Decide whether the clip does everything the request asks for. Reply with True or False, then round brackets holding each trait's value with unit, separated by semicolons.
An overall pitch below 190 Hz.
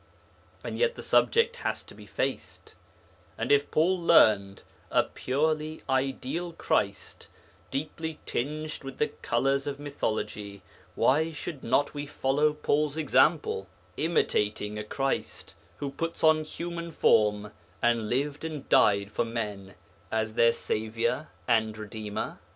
True (135 Hz)